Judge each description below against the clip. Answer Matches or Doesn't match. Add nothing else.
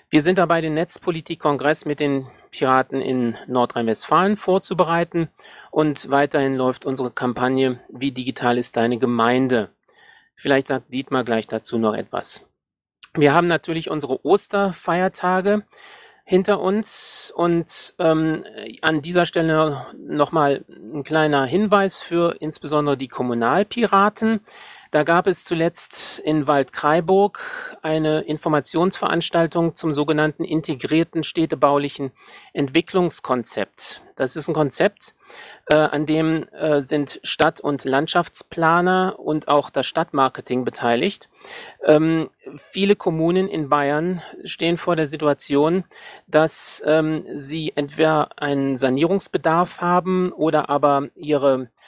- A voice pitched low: Doesn't match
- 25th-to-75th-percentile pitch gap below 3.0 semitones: Doesn't match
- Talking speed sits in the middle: Doesn't match